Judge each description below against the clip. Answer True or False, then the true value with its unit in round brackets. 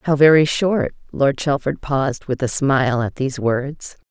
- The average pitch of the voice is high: False (140 Hz)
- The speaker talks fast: False (175 wpm)